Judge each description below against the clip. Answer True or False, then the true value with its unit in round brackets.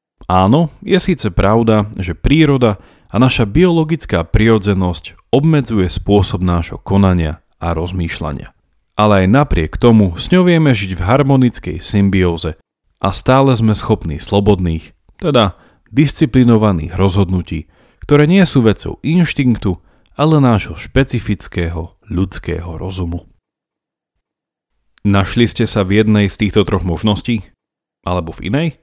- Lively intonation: True (5.9 semitones)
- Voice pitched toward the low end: True (100 Hz)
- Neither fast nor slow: True (120 wpm)